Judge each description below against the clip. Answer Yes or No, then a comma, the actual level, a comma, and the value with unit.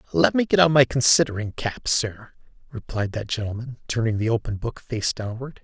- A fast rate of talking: No, average, 180 wpm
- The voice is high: No, low, 115 Hz